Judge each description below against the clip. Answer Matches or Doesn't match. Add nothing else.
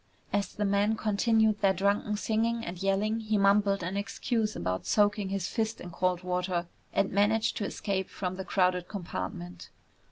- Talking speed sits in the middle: Matches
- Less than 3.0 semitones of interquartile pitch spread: Matches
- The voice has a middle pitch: Doesn't match